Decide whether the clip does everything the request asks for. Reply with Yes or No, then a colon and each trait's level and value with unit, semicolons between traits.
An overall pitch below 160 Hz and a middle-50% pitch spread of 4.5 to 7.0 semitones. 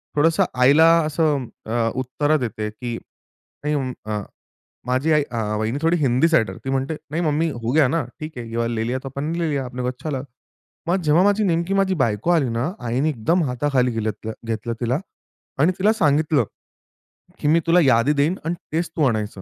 Yes: medium, 140 Hz; average, 5.0 semitones